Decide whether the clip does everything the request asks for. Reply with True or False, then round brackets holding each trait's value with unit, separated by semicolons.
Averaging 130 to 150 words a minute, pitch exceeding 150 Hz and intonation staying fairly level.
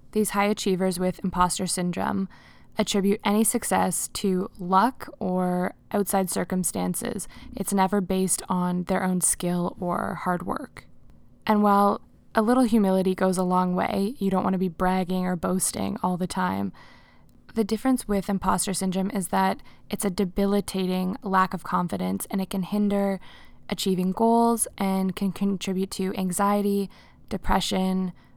True (145 wpm; 190 Hz; 1.6 semitones)